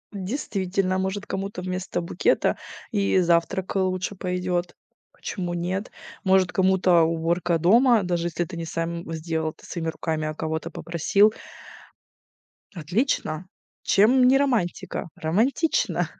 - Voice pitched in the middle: Yes, medium, 180 Hz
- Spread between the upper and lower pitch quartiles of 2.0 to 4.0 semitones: Yes, average, 2.7 semitones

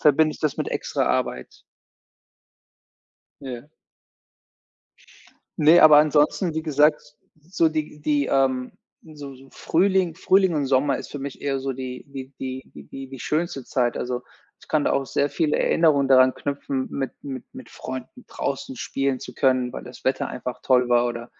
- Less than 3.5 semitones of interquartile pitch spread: Yes, average, 2.7 semitones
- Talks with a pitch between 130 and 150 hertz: Yes, low, 135 Hz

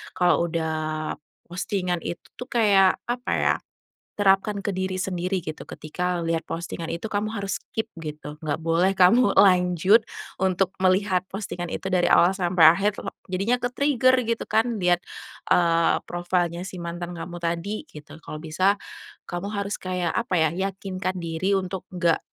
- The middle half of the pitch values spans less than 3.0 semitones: Yes, narrow, 2.6 semitones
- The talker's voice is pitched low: No, medium, 185 Hz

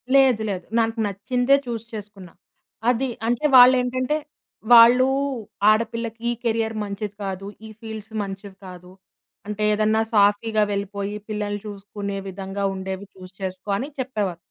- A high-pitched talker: Yes, high, 210 Hz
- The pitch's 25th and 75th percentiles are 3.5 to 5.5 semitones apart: No, average, 2.7 semitones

